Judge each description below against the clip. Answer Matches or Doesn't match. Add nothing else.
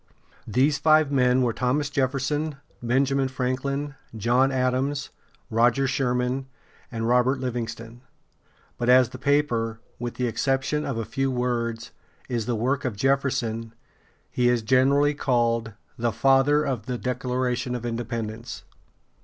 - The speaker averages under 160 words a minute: Matches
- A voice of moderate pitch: Doesn't match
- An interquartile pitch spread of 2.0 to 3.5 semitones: Matches